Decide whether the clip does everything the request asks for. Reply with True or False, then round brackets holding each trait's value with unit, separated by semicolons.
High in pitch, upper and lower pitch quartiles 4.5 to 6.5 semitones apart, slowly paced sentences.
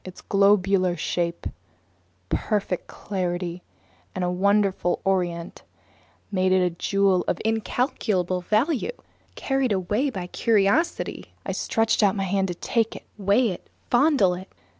False (195 Hz; 3.2 semitones; 125 wpm)